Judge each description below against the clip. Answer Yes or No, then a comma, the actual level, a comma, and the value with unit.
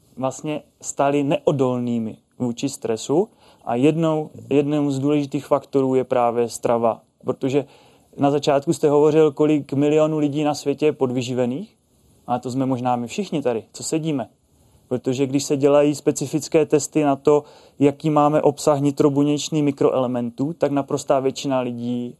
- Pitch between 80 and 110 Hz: No, medium, 140 Hz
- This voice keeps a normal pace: Yes, average, 140 wpm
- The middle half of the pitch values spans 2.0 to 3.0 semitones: Yes, average, 2.7 semitones